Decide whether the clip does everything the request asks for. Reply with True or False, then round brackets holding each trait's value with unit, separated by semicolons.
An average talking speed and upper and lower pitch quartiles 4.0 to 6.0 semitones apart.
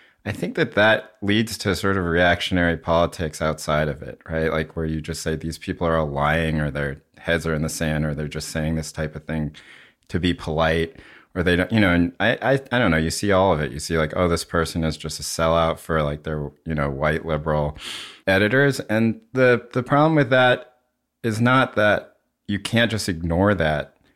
False (225 wpm; 4.7 semitones)